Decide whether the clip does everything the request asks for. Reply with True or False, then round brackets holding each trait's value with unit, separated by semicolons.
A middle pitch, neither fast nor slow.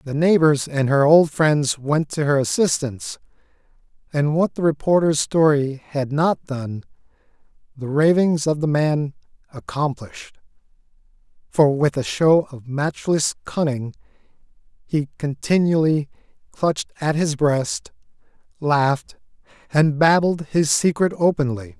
False (150 Hz; 120 wpm)